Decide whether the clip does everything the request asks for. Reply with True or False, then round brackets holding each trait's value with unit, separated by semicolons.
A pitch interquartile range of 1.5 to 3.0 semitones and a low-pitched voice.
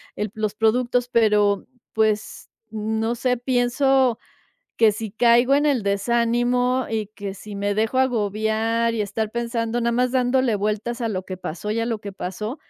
False (2.5 semitones; 225 Hz)